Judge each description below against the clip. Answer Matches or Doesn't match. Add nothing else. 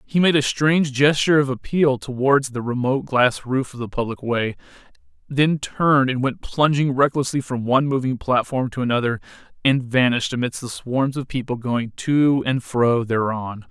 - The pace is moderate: Matches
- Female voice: Doesn't match